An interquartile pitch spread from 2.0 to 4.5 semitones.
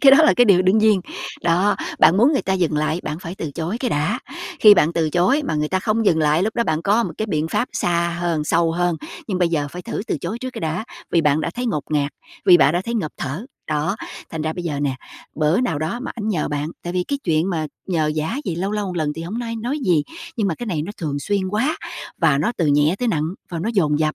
No: average, 5.3 semitones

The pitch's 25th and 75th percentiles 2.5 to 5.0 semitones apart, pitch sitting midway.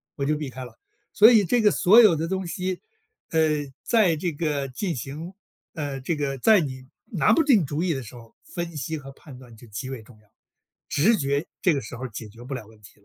No: wide, 5.5 semitones; medium, 150 Hz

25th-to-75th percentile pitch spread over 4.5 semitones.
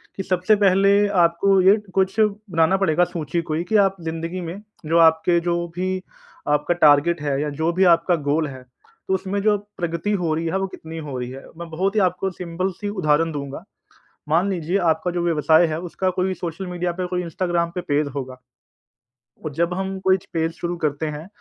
No: average, 3.0 semitones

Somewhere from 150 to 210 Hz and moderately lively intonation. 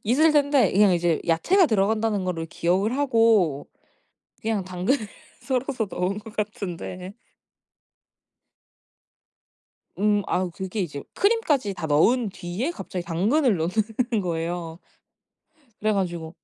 Yes: high, 200 Hz; average, 4.8 semitones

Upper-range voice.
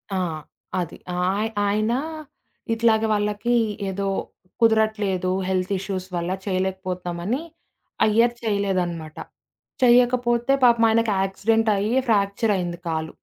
Yes: high, 205 Hz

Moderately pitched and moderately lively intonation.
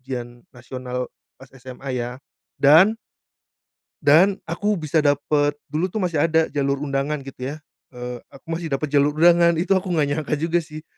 Yes: medium, 145 Hz; average, 3.9 semitones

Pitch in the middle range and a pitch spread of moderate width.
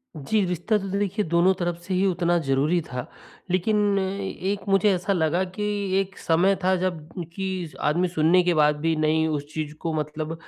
Yes: medium, 175 Hz; average, 3.4 semitones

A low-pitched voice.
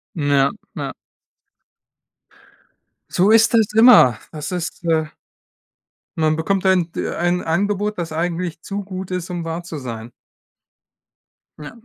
No: medium, 175 Hz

